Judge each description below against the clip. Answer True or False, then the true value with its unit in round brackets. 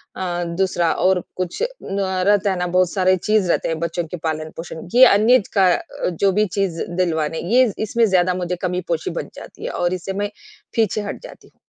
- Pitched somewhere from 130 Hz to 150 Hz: False (185 Hz)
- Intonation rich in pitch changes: False (2.8 semitones)